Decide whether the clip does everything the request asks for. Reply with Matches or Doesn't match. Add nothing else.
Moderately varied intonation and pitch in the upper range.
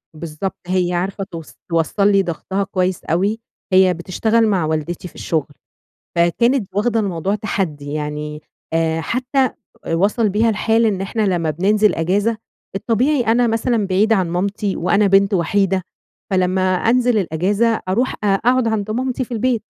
Matches